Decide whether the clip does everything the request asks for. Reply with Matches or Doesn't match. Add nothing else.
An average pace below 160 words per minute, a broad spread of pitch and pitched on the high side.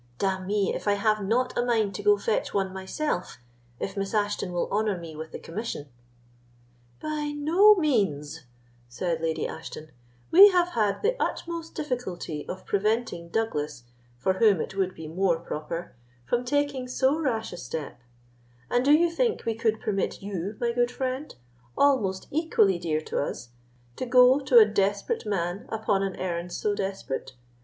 Doesn't match